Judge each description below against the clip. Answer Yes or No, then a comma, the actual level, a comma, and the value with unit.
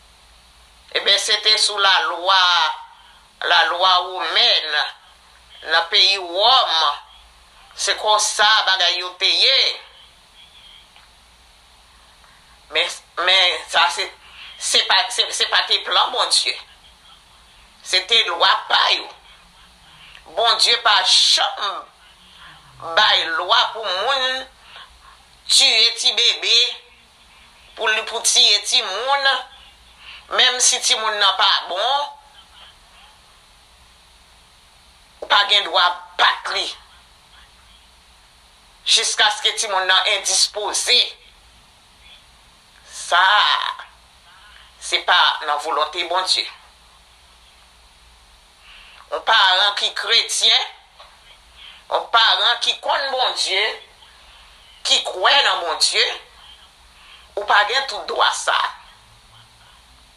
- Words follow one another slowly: Yes, slow, 95 wpm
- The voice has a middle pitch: Yes, medium, 175 Hz